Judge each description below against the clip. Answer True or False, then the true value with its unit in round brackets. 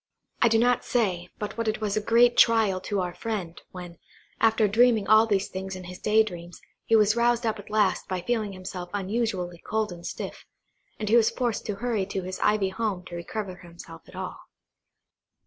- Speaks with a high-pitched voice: True (210 Hz)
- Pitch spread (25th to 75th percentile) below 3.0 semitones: False (3.3 semitones)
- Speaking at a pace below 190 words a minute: False (200 wpm)